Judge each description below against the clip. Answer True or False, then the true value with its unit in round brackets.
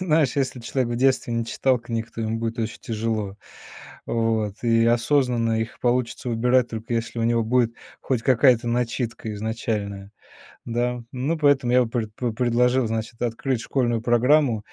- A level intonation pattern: True (1.8 semitones)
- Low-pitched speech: True (120 Hz)